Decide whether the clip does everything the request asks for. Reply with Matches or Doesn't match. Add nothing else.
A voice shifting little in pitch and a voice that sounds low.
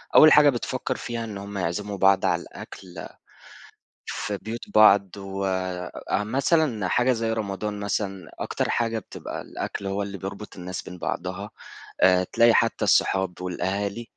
Doesn't match